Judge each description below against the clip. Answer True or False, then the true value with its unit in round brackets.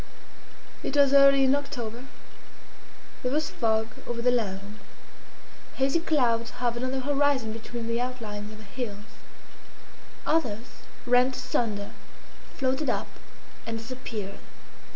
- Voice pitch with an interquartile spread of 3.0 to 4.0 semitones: True (3.3 semitones)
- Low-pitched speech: False (245 Hz)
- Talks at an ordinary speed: False (120 wpm)